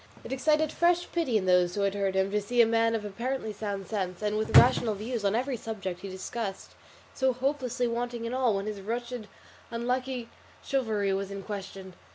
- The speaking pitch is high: Yes, high, 225 Hz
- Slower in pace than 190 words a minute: No, average, 200 wpm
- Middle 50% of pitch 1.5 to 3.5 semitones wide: No, average, 3.9 semitones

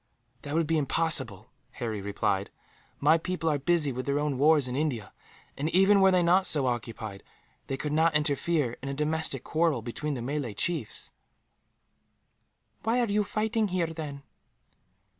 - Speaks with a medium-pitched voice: Yes, medium, 150 Hz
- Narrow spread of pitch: No, average, 4.6 semitones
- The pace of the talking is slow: No, average, 160 wpm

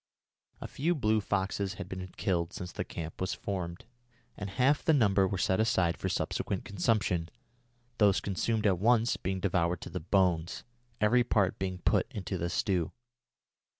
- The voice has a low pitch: Yes, very low, 95 Hz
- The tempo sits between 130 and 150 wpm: No, average, 165 wpm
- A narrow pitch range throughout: No, average, 3.0 semitones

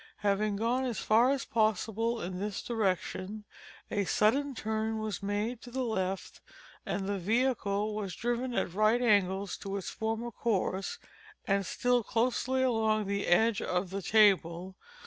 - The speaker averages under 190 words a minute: Yes, average, 150 wpm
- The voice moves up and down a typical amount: Yes, average, 3.0 semitones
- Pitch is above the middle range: Yes, high, 215 Hz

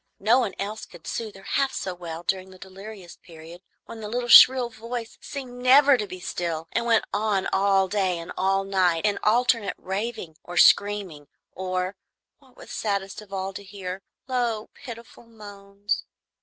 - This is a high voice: Yes, high, 200 Hz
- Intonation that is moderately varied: Yes, average, 3.6 semitones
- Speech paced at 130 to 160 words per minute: No, average, 170 wpm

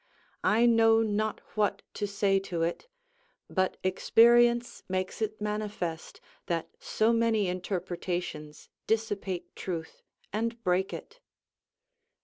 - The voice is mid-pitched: No, high, 205 Hz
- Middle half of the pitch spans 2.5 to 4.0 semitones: Yes, average, 3.5 semitones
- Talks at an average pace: No, slow, 110 wpm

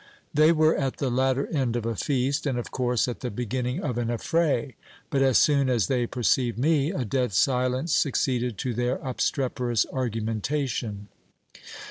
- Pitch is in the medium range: No, low, 125 Hz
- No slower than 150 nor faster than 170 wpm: Yes, average, 165 wpm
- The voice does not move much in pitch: Yes, narrow, 2.3 semitones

